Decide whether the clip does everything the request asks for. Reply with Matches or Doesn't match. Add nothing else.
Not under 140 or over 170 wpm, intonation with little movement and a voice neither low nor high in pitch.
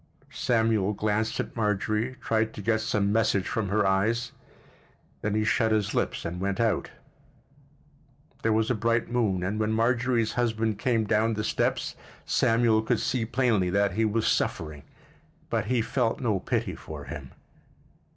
Doesn't match